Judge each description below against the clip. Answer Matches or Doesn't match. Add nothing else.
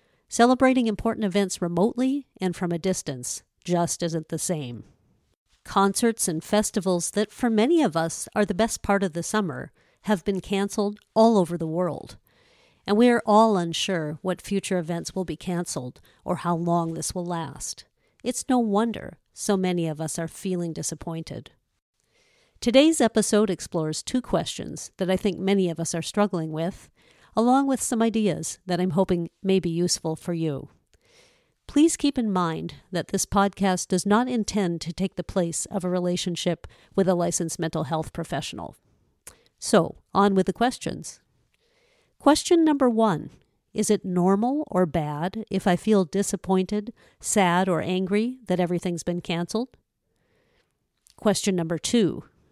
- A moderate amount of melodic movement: Matches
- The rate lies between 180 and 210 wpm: Doesn't match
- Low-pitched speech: Doesn't match